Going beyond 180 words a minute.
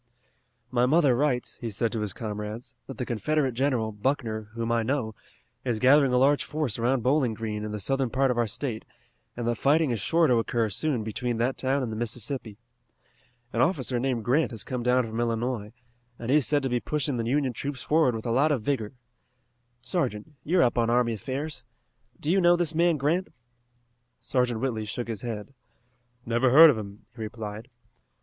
Yes: average, 200 wpm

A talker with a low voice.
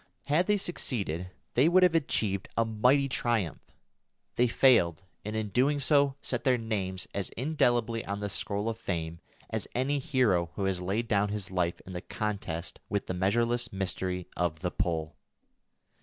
Yes: low, 105 Hz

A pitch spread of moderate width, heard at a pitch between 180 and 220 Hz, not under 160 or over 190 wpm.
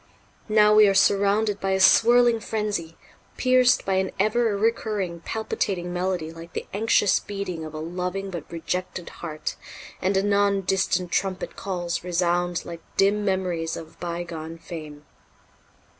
No: average, 3.1 semitones; high, 190 Hz; average, 140 wpm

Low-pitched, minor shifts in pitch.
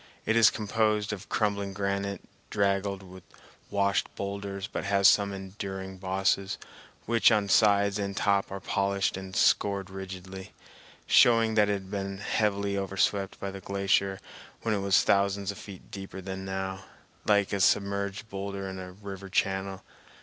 Yes: low, 100 Hz; narrow, 0.8 semitones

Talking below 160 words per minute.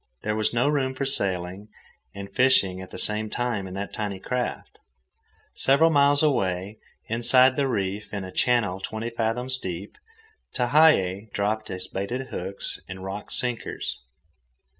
Yes: average, 145 wpm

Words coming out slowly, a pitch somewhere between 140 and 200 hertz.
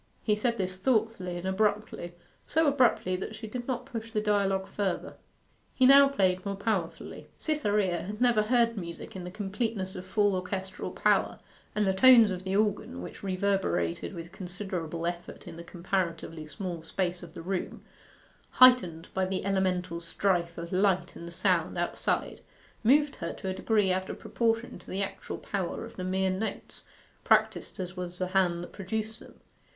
No: average, 175 wpm; high, 190 Hz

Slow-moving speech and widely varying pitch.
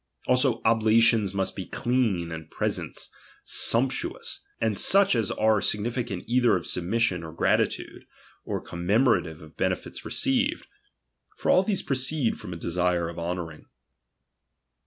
Yes: slow, 130 wpm; wide, 6.2 semitones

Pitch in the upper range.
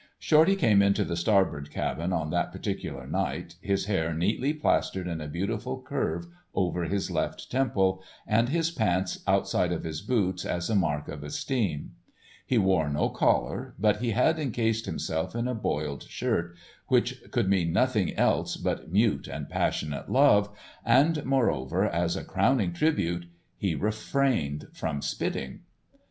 No: low, 100 Hz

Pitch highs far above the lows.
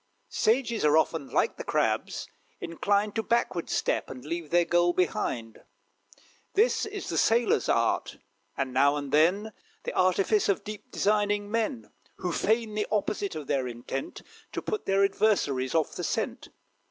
Yes: wide, 6.0 semitones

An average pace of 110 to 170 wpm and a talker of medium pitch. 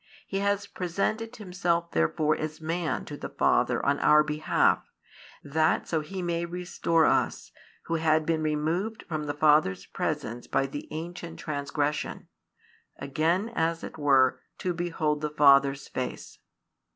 Yes: average, 140 wpm; medium, 155 Hz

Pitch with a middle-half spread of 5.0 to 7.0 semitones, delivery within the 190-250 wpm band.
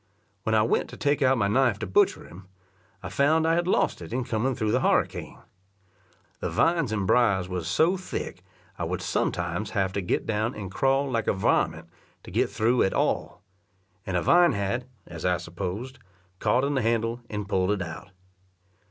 Yes: wide, 5.5 semitones; average, 195 wpm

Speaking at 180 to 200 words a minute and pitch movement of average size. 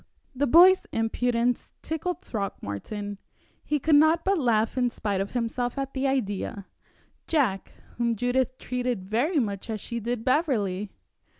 No: average, 140 wpm; average, 4.4 semitones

